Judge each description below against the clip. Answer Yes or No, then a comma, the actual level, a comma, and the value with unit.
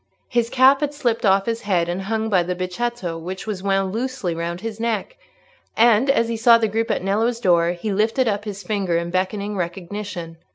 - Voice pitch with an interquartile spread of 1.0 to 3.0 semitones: No, average, 4.0 semitones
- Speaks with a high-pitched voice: Yes, high, 205 Hz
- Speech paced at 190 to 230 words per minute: Yes, fast, 205 wpm